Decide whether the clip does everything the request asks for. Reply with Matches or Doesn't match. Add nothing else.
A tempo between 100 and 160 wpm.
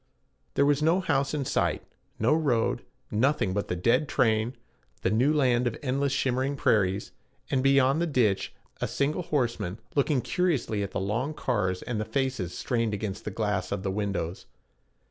Doesn't match